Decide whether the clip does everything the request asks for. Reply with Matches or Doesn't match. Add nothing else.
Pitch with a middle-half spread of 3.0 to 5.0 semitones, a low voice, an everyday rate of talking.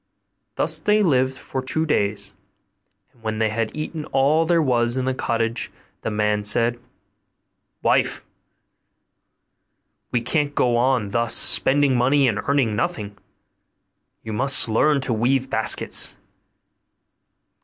Doesn't match